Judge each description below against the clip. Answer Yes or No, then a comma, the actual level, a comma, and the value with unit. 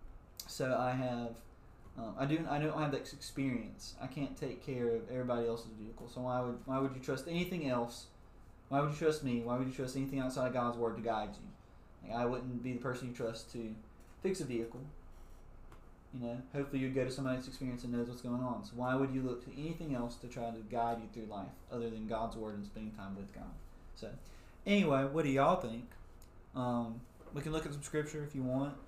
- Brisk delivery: Yes, fast, 230 wpm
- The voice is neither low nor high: No, low, 125 Hz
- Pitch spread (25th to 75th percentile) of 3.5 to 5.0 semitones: No, average, 2.9 semitones